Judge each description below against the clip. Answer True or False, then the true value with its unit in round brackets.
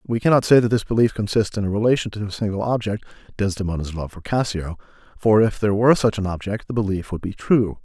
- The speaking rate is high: True (230 wpm)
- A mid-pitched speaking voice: False (105 Hz)